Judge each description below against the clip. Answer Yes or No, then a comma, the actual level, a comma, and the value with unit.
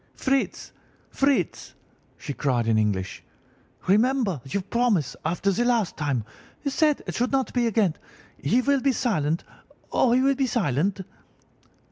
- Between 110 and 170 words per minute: Yes, average, 145 wpm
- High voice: Yes, high, 215 Hz